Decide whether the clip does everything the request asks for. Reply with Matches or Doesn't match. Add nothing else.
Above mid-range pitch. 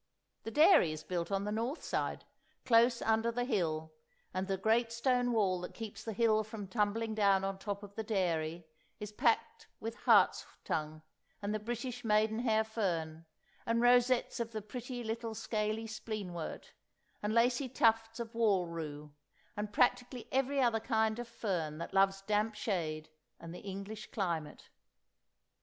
Matches